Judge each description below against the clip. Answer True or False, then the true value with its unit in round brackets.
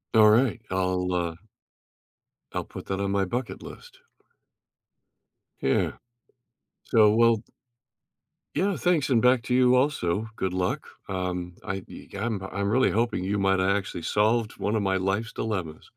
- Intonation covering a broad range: False (3.9 semitones)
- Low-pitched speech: True (100 Hz)